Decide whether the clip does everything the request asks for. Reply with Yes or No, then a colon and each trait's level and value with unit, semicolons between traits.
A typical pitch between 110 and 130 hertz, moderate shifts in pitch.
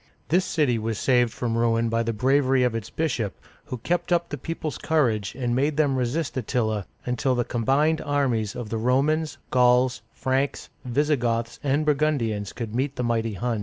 Yes: low, 125 Hz; average, 3.9 semitones